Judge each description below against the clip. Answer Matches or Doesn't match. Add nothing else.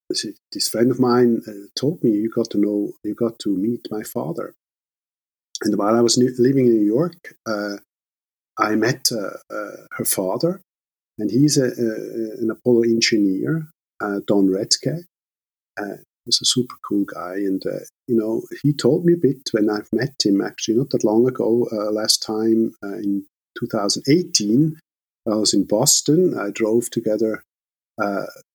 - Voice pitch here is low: Matches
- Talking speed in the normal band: Matches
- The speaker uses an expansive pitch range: Doesn't match